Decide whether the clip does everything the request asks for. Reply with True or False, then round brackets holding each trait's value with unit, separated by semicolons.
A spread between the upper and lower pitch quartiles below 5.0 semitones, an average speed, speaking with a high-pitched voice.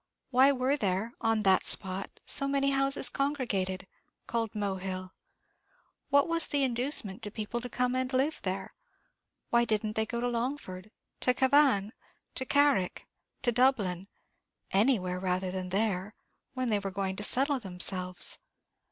False (5.5 semitones; 145 wpm; 225 Hz)